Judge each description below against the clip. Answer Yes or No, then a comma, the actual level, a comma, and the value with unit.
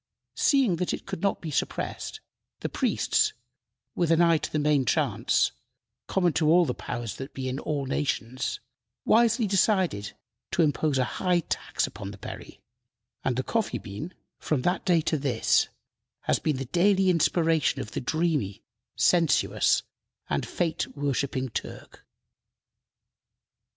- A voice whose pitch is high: No, medium, 155 Hz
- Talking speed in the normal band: Yes, average, 145 wpm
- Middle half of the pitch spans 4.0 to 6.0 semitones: Yes, average, 5.2 semitones